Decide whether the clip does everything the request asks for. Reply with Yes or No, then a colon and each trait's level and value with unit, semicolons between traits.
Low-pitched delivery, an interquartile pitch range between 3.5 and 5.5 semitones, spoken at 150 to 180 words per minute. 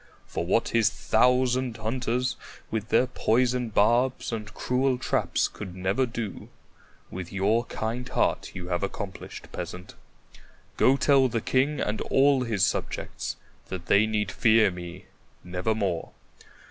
No: low, 110 Hz; average, 4.5 semitones; slow, 135 wpm